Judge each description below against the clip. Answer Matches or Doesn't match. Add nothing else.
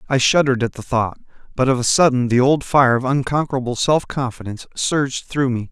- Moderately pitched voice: Doesn't match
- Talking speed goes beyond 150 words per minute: Matches